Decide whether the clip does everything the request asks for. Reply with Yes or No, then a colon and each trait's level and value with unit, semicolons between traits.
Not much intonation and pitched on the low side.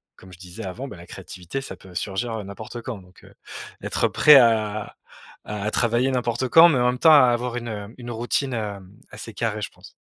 No: average, 3.5 semitones; low, 115 Hz